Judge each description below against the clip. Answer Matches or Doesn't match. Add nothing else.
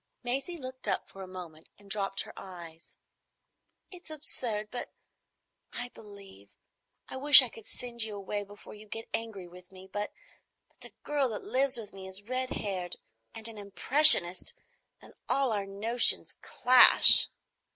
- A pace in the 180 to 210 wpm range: Doesn't match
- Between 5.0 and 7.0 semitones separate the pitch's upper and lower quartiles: Doesn't match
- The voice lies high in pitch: Matches